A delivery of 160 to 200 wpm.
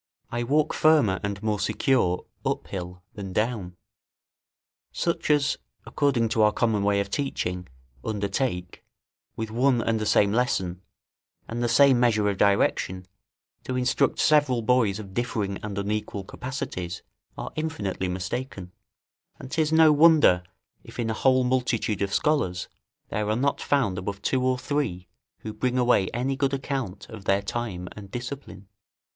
No: average, 150 wpm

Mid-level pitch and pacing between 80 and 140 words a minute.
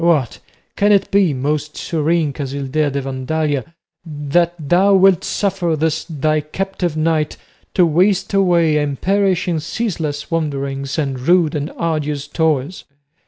Yes: medium, 155 Hz; slow, 135 wpm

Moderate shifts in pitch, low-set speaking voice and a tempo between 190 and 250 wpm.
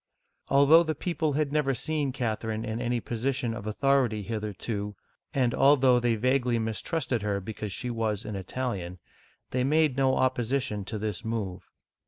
No: average, 4.1 semitones; low, 120 Hz; average, 155 wpm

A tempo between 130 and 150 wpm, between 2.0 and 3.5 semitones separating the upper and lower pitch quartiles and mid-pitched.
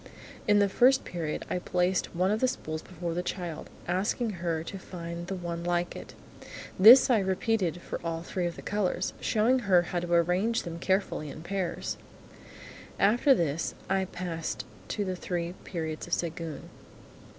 No: average, 170 wpm; narrow, 2.6 semitones; medium, 180 Hz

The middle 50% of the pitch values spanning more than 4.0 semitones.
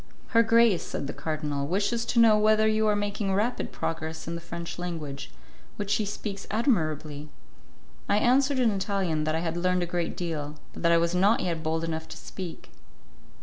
Yes: average, 4.8 semitones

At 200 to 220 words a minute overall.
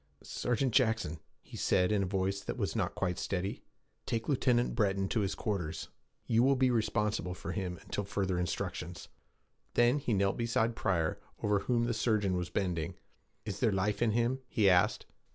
No: average, 175 wpm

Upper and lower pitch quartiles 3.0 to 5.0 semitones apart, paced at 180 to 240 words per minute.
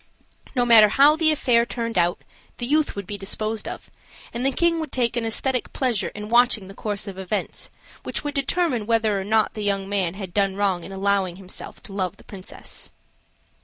Yes: average, 3.9 semitones; average, 200 wpm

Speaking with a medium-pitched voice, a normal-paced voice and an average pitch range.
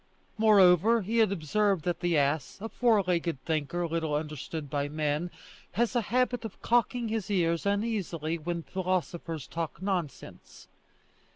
Yes: medium, 175 Hz; average, 145 wpm; average, 5.0 semitones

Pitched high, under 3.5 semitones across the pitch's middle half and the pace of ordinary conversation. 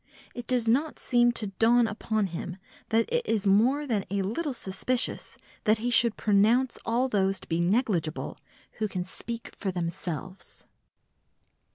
No: high, 220 Hz; average, 3.9 semitones; average, 155 wpm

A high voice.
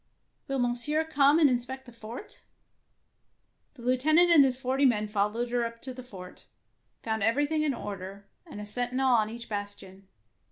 Yes: high, 245 Hz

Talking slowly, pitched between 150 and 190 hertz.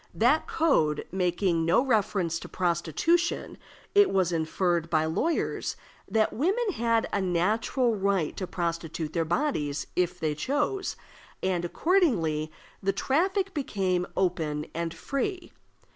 Yes: slow, 125 wpm; medium, 185 Hz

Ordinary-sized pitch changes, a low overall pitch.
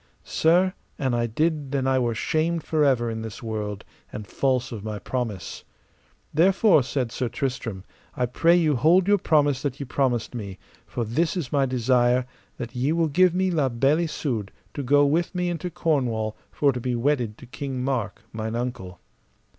Yes: average, 4.8 semitones; low, 130 Hz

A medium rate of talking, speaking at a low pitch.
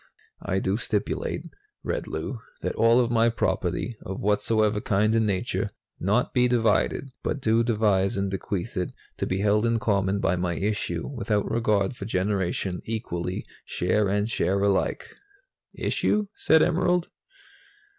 Yes: average, 145 wpm; low, 105 Hz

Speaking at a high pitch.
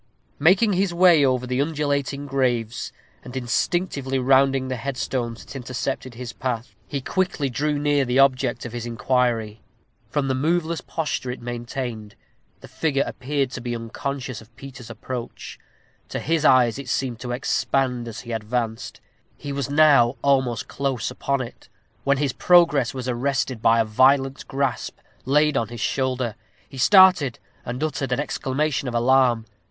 No: low, 130 Hz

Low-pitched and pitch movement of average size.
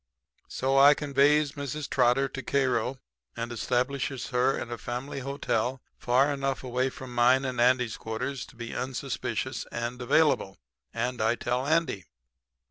No: low, 130 Hz; narrow, 2.1 semitones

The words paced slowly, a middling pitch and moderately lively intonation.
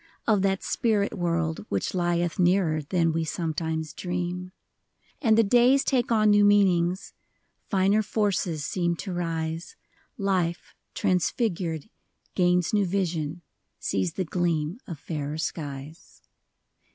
Yes: slow, 120 wpm; medium, 175 Hz; average, 3.5 semitones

